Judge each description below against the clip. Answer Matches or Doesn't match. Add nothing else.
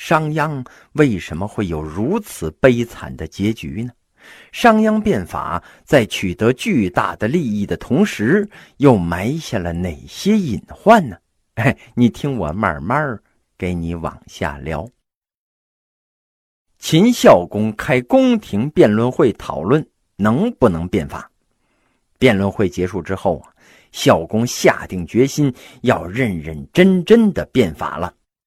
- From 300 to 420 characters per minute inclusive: Doesn't match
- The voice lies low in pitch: Matches